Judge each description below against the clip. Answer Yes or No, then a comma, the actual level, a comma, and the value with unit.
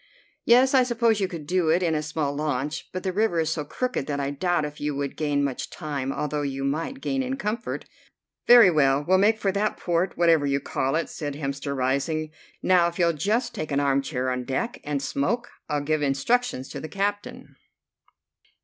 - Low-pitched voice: No, medium, 155 Hz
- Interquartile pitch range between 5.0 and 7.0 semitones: Yes, wide, 5.6 semitones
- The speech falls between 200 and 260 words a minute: Yes, fast, 205 wpm